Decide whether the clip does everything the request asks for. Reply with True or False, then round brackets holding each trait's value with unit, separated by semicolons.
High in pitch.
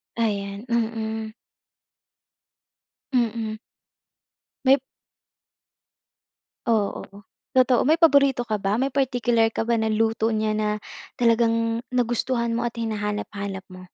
True (230 Hz)